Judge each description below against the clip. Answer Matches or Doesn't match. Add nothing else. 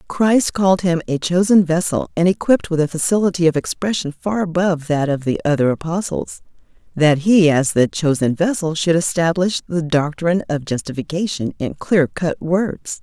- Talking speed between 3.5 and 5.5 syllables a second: Matches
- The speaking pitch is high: Doesn't match